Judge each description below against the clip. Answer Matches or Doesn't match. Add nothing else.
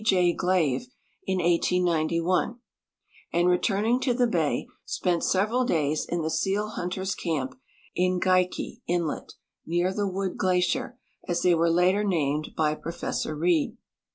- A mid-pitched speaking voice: Matches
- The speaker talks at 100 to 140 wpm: Matches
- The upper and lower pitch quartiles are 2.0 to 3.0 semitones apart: Matches